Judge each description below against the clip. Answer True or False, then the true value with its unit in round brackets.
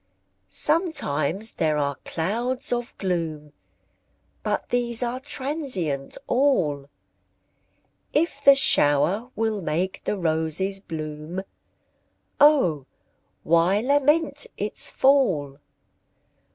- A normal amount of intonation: False (9.0 semitones)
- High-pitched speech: True (195 Hz)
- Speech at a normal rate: False (85 wpm)